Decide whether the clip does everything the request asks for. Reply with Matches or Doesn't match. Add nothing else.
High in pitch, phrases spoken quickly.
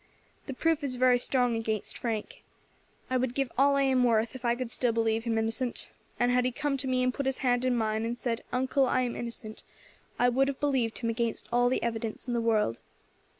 Matches